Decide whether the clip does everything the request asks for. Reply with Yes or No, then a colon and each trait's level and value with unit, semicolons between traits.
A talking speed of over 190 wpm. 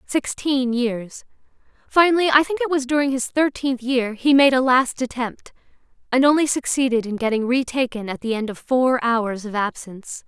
No: average, 175 wpm